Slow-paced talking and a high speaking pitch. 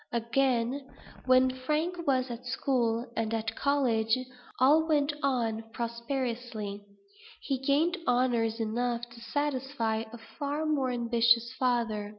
Yes: slow, 120 wpm; high, 245 Hz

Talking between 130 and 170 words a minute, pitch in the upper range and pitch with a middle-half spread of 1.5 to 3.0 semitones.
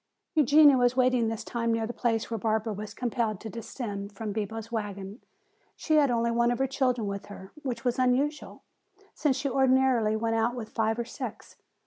No: average, 190 wpm; high, 235 Hz; average, 2.7 semitones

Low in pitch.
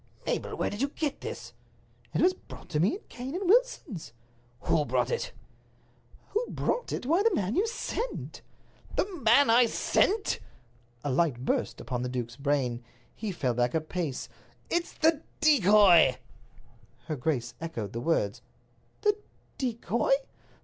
No: high, 200 Hz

